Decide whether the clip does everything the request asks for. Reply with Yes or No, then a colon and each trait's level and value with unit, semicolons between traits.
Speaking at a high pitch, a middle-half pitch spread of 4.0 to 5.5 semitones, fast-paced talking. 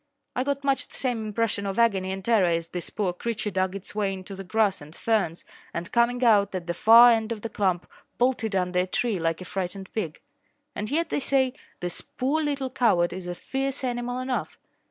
Yes: high, 210 Hz; average, 4.8 semitones; fast, 215 wpm